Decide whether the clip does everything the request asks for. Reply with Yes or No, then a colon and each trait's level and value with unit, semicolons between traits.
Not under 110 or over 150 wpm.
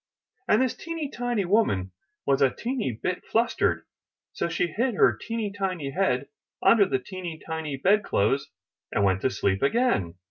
No: average, 175 wpm